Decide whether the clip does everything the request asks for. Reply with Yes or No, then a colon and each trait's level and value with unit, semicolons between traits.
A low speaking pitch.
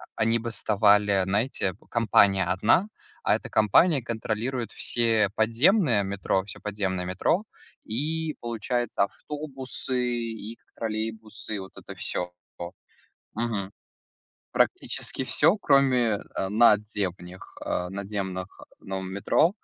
Yes: low, 110 Hz